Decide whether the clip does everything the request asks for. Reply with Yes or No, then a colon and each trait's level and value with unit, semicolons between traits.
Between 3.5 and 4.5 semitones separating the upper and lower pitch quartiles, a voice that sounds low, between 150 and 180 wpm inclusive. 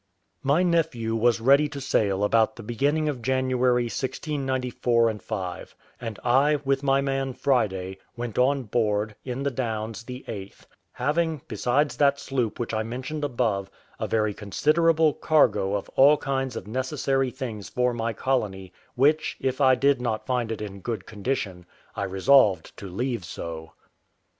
Yes: average, 4.1 semitones; low, 125 Hz; average, 155 wpm